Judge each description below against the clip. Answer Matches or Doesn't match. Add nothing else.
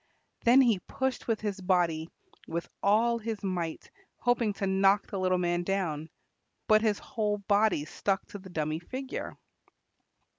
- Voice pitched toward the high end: Matches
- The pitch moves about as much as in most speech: Matches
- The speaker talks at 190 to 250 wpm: Doesn't match